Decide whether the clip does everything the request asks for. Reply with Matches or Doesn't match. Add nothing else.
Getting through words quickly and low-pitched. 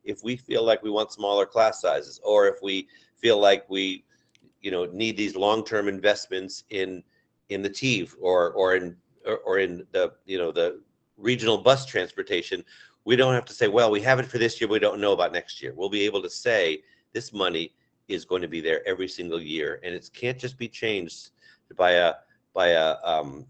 Matches